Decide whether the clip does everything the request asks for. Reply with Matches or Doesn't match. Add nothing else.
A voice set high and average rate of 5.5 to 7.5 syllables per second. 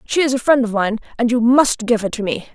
Matches